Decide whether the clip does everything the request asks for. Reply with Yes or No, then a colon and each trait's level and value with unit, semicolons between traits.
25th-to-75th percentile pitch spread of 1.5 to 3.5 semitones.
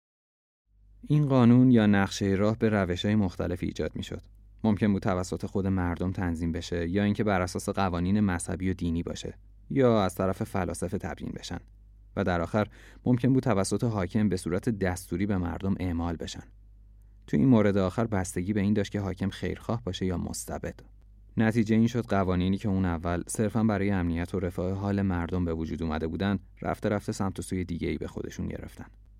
Yes: narrow, 2.5 semitones